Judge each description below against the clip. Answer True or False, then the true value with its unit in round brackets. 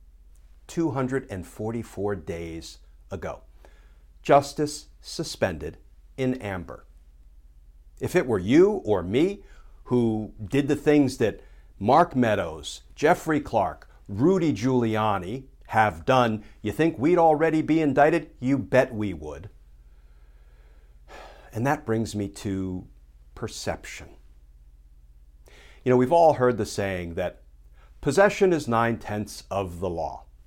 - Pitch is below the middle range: True (100 Hz)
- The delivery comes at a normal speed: False (110 wpm)